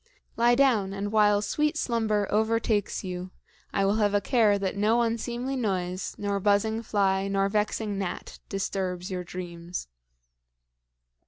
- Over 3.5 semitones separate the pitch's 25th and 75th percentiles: No, narrow, 2.4 semitones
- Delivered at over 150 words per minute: No, average, 140 wpm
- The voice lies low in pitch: No, high, 205 Hz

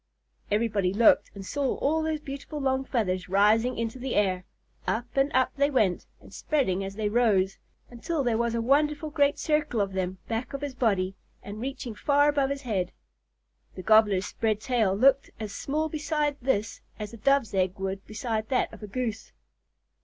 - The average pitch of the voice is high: Yes, high, 230 Hz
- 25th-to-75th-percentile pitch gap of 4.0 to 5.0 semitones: No, wide, 5.4 semitones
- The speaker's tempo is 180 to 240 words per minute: Yes, average, 185 wpm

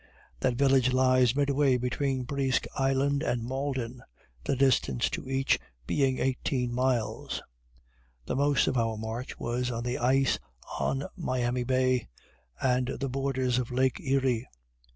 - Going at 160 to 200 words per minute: No, slow, 135 wpm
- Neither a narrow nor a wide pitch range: No, narrow, 1.6 semitones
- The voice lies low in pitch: Yes, low, 130 Hz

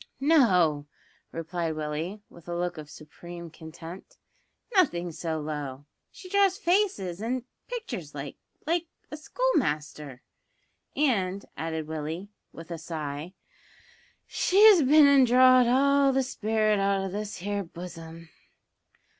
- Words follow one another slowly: Yes, slow, 120 wpm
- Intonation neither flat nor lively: No, wide, 8.3 semitones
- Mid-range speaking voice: Yes, medium, 180 Hz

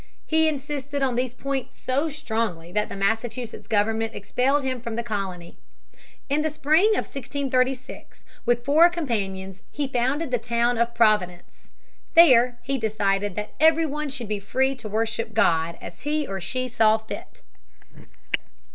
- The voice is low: No, high, 240 Hz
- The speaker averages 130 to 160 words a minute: Yes, average, 155 wpm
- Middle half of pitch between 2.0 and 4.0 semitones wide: No, average, 4.5 semitones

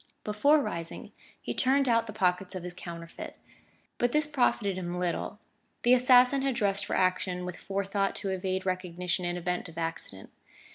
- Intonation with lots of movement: No, average, 4.9 semitones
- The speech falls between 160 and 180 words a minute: Yes, average, 170 wpm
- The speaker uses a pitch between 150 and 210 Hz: Yes, high, 190 Hz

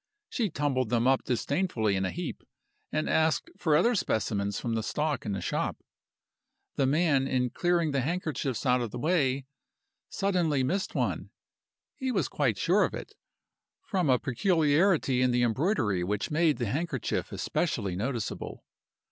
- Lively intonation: Yes, wide, 5.7 semitones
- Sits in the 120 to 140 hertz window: Yes, low, 135 Hz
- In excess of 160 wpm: No, average, 155 wpm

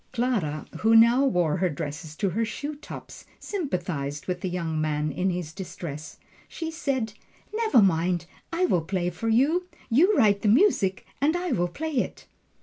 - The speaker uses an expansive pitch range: Yes, wide, 8.2 semitones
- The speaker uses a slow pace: No, average, 170 wpm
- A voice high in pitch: Yes, high, 195 Hz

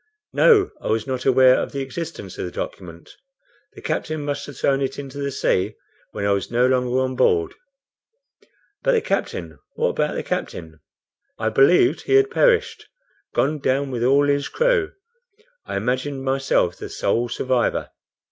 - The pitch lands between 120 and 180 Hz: Yes, low, 135 Hz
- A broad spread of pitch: No, average, 4.2 semitones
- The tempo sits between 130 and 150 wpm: No, average, 165 wpm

